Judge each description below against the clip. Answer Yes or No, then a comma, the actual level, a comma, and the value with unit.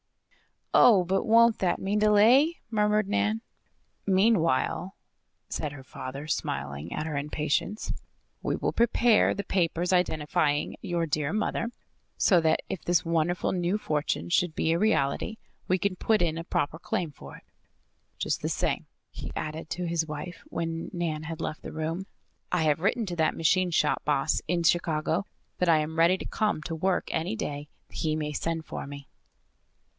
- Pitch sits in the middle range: Yes, medium, 170 Hz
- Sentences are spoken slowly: No, average, 170 wpm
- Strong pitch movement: No, average, 3.8 semitones